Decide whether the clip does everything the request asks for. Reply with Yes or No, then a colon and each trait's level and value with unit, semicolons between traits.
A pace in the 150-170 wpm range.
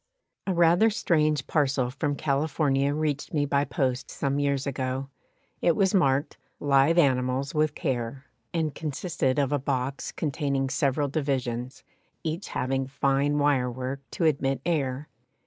No: average, 140 wpm